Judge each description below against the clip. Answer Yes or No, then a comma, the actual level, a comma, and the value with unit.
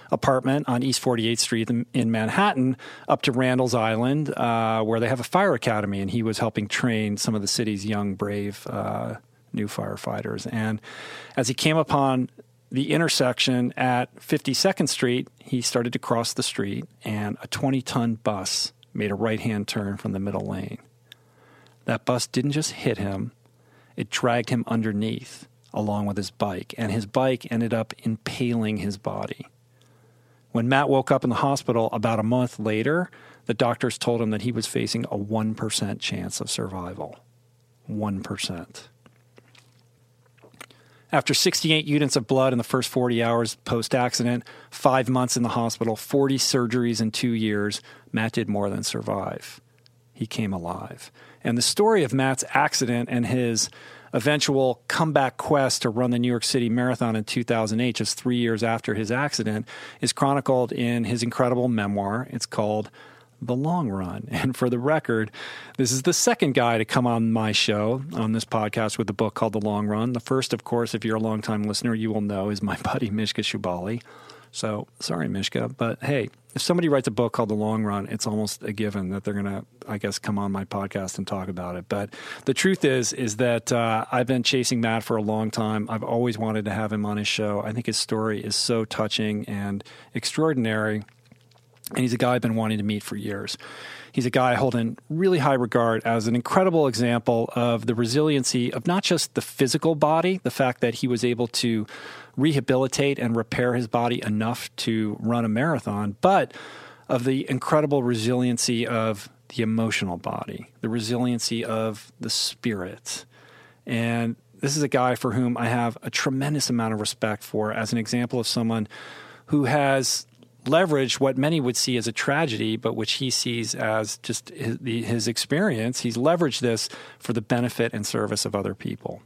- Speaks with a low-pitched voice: Yes, low, 120 Hz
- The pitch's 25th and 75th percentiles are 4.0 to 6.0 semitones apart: No, average, 2.7 semitones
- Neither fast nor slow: Yes, average, 180 wpm